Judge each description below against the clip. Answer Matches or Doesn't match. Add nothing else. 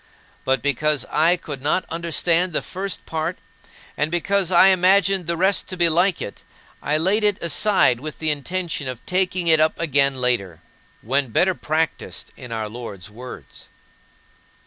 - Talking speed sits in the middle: Matches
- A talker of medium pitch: Matches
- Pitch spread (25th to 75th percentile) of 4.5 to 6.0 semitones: Matches